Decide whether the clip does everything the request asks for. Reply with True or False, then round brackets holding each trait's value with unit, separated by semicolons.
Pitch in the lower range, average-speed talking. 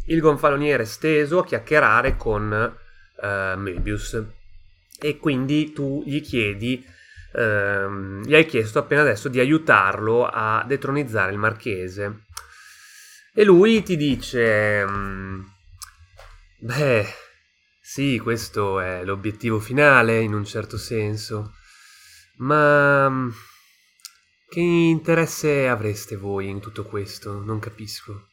False (110 Hz; 110 wpm)